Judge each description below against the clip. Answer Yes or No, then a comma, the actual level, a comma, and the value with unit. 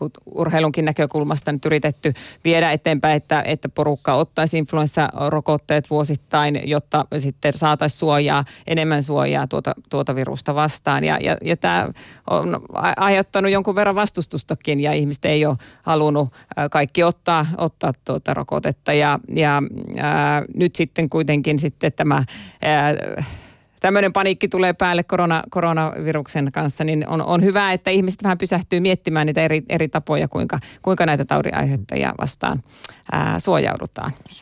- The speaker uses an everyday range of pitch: No, narrow, 2.3 semitones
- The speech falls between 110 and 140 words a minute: Yes, average, 135 wpm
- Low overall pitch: No, medium, 155 Hz